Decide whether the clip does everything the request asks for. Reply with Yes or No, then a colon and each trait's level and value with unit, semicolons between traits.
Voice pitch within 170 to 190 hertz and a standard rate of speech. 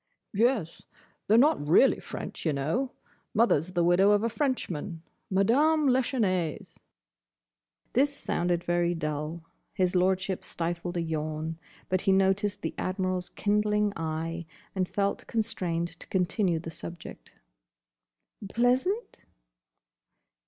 No: medium, 185 Hz; slow, 115 wpm